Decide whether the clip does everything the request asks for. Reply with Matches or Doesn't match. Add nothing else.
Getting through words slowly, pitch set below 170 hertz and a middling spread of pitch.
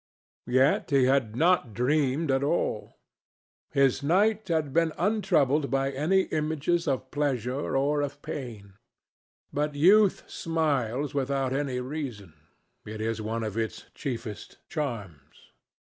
Matches